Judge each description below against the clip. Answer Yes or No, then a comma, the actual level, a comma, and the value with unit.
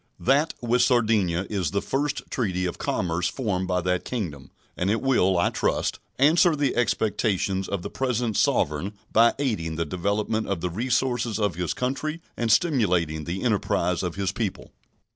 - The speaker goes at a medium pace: Yes, average, 165 wpm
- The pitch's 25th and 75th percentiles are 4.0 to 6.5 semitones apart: Yes, wide, 5.4 semitones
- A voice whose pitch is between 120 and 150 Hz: No, low, 100 Hz